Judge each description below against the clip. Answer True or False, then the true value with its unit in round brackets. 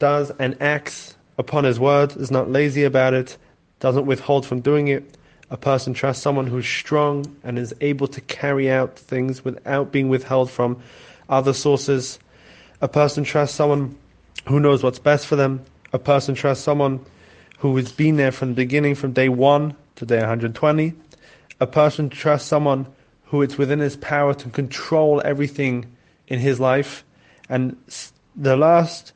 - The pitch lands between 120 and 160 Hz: True (140 Hz)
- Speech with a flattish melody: True (2.0 semitones)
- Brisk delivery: False (170 wpm)